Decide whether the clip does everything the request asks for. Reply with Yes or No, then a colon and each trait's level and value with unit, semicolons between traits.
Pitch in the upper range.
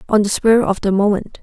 Yes: high, 205 Hz